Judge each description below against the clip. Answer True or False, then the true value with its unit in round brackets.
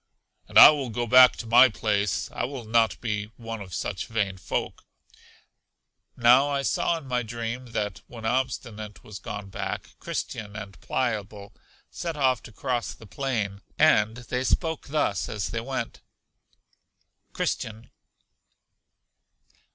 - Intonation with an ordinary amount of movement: True (3.3 semitones)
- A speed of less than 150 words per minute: True (140 wpm)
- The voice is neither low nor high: False (115 Hz)